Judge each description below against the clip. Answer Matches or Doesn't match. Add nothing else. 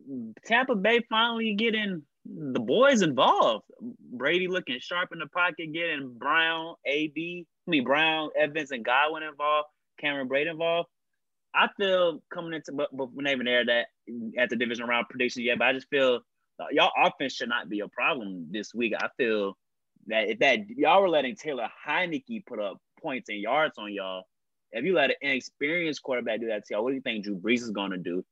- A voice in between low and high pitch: Matches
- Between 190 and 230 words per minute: Matches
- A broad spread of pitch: Matches